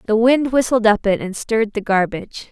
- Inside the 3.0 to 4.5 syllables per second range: No, 5.6 syllables/s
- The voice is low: No, high, 220 Hz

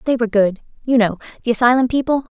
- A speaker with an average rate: Yes, average, 180 wpm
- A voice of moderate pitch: No, high, 235 Hz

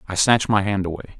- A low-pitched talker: Yes, low, 100 Hz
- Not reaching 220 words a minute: No, fast, 250 wpm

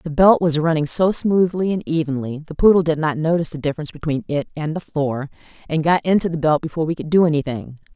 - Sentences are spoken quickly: Yes, fast, 225 wpm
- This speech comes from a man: No, female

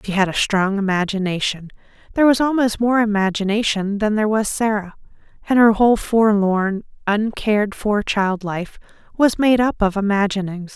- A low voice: No, high, 210 Hz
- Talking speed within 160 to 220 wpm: No, average, 150 wpm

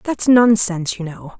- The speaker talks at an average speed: Yes, average, 170 wpm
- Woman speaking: Yes, female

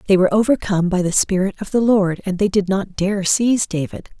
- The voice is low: No, high, 195 Hz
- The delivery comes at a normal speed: No, fast, 230 wpm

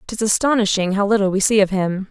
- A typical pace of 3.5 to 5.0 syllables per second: No, 6.0 syllables/s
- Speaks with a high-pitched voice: Yes, high, 205 Hz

